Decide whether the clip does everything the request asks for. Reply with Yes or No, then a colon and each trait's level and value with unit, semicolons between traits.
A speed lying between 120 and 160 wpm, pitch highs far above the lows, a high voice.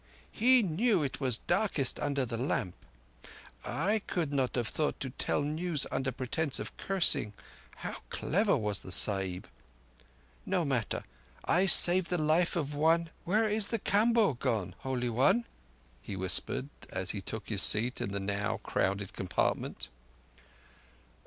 No: average, 150 wpm; wide, 8.4 semitones; medium, 140 Hz